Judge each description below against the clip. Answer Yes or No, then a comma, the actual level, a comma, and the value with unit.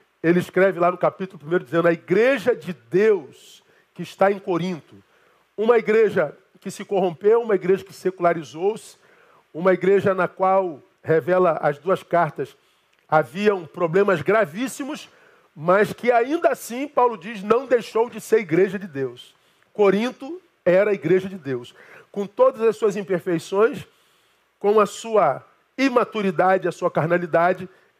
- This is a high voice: Yes, high, 195 Hz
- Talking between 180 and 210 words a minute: No, average, 140 wpm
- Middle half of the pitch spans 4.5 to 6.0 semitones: No, average, 3.9 semitones